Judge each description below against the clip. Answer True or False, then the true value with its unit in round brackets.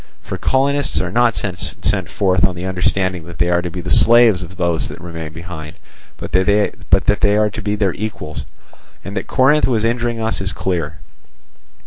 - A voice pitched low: True (95 Hz)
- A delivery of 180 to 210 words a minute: True (185 wpm)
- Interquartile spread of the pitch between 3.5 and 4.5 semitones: True (4.1 semitones)